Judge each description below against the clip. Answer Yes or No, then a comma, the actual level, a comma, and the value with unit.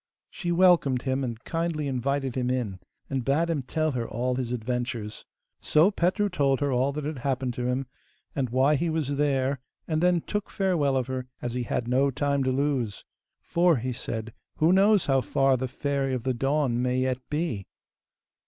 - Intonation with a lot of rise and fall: No, average, 3.3 semitones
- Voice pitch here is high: No, low, 135 Hz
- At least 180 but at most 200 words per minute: Yes, average, 190 wpm